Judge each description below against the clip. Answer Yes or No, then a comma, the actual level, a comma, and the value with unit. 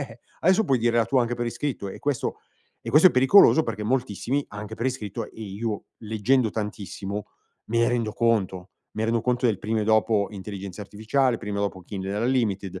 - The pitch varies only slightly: No, average, 3.1 semitones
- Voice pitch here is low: Yes, low, 110 Hz